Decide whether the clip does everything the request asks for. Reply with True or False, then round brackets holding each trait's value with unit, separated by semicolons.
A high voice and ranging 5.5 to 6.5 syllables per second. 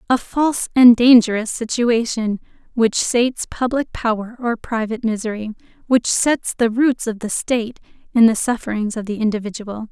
False (230 Hz; 5.0 syllables/s)